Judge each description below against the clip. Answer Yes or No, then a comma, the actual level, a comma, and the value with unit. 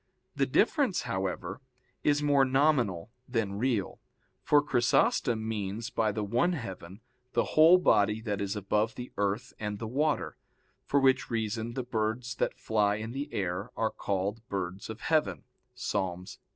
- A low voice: Yes, low, 110 Hz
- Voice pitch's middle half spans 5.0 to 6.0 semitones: No, average, 4.3 semitones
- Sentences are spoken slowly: No, average, 150 wpm